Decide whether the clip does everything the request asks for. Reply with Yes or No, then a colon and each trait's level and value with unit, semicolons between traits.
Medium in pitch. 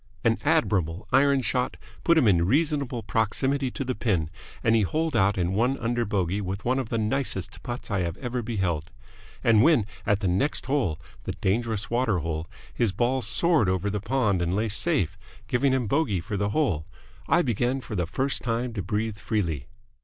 No: low, 110 Hz